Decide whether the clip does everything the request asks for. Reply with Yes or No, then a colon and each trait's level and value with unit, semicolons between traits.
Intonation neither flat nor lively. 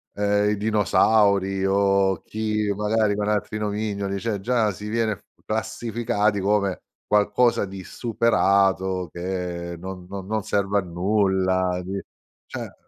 No: narrow, 2.0 semitones